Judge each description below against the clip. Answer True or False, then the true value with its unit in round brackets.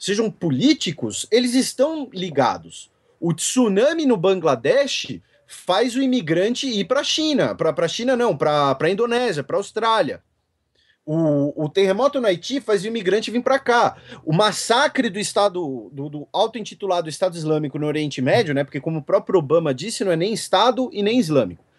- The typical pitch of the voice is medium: False (200 Hz)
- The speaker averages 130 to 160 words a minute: False (175 wpm)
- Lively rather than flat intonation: True (7.4 semitones)